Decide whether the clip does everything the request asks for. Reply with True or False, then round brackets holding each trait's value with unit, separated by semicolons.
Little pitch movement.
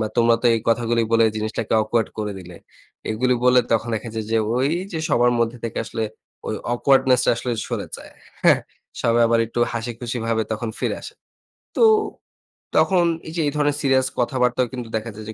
True (2.0 semitones)